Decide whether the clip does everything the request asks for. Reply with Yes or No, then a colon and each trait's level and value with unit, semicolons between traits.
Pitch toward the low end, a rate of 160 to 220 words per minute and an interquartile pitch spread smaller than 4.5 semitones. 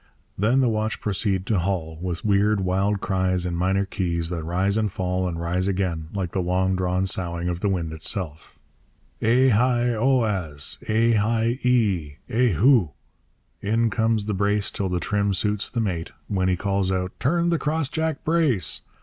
Yes: low, 100 Hz; average, 175 wpm; average, 3.7 semitones